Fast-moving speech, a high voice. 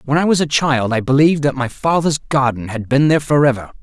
No: fast, 250 wpm; medium, 140 Hz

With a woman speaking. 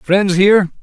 No: male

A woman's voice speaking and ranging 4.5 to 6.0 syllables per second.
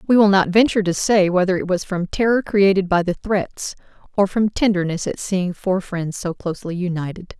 Yes: female; 5.3 syllables/s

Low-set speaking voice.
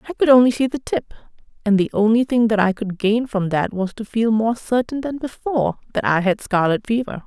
No: high, 225 Hz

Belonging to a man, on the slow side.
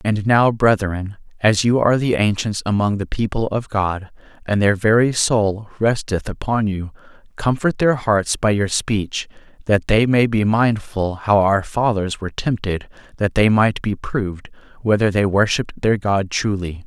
No: male; average, 165 wpm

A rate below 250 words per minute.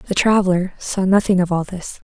Yes: average, 200 wpm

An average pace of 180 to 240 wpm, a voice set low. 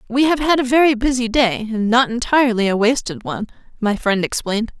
No: average, 200 wpm; high, 240 Hz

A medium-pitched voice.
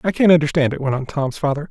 Yes: medium, 150 Hz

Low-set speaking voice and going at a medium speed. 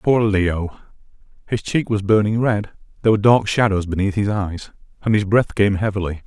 Yes: low, 105 Hz; average, 180 wpm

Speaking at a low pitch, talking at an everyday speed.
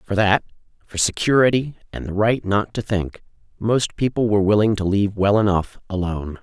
Yes: low, 105 Hz; average, 180 wpm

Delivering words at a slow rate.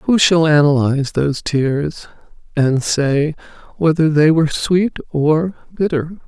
Yes: slow, 125 wpm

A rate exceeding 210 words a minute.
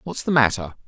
No: fast, 205 wpm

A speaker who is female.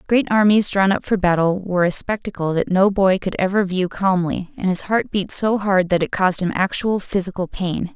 Yes: female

